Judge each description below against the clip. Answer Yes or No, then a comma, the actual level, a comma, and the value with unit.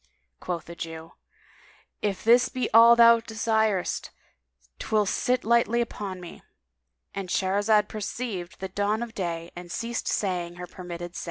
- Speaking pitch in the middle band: No, high, 205 Hz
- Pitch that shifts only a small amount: No, average, 4.3 semitones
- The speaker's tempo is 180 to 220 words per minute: No, slow, 135 wpm